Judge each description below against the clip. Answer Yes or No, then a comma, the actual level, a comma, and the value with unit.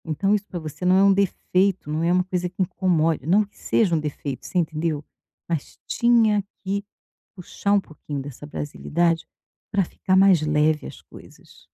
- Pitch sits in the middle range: Yes, medium, 175 Hz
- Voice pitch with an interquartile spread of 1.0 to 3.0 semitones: No, average, 4.0 semitones